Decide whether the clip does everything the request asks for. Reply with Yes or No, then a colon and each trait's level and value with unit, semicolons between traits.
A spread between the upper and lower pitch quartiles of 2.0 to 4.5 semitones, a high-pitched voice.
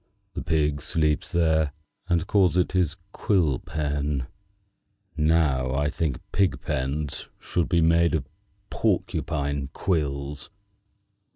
No: average, 2.9 semitones; very low, 75 Hz